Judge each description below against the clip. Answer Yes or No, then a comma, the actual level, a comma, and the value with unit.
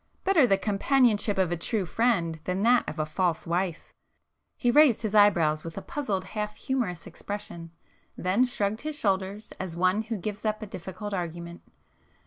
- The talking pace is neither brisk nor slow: Yes, average, 165 wpm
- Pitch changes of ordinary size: Yes, average, 4.2 semitones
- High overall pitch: Yes, high, 200 Hz